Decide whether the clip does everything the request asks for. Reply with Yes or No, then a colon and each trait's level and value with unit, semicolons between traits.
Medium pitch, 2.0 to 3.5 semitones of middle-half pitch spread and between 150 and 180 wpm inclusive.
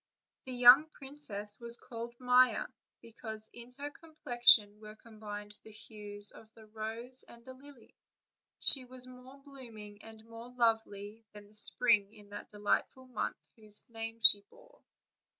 No: high, 230 Hz; average, 2.9 semitones; average, 155 wpm